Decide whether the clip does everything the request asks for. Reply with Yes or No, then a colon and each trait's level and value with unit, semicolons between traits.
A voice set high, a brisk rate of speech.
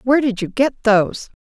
Yes: high, 235 Hz; fast, 210 wpm